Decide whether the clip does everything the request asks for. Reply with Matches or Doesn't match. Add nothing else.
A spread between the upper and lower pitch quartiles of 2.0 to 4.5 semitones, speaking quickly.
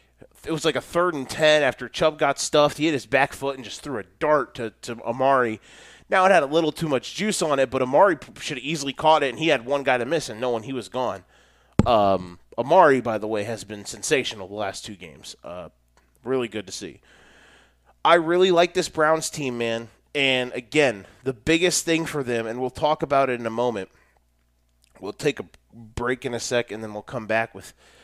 Doesn't match